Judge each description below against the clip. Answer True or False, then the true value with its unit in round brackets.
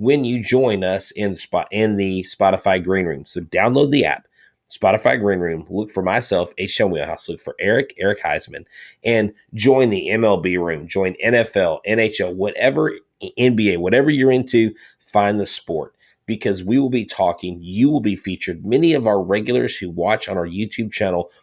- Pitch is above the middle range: False (105 Hz)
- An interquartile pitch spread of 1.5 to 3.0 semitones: False (3.8 semitones)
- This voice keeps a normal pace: True (175 wpm)